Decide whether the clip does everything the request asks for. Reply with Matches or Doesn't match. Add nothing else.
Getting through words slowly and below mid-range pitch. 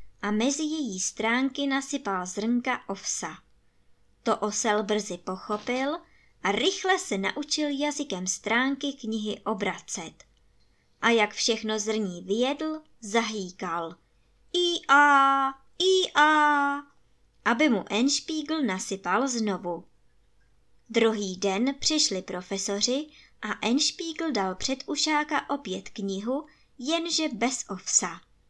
Doesn't match